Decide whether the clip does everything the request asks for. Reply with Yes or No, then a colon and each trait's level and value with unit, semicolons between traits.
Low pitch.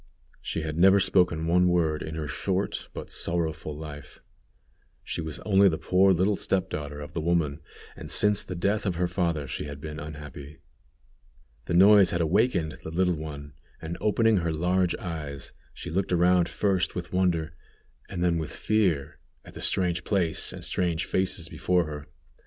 Yes: very low, 85 Hz